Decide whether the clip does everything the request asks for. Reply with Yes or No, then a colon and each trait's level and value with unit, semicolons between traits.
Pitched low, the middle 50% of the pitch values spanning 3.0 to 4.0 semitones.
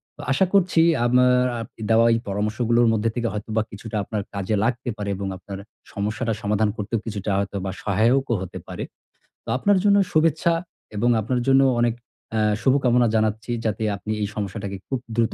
Yes: low, 110 Hz; average, 3.3 semitones